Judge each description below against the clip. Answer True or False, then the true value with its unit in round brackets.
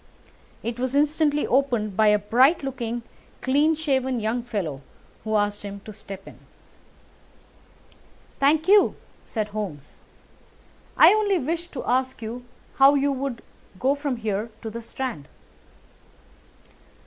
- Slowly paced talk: True (130 wpm)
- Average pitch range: True (4.8 semitones)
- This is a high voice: True (250 Hz)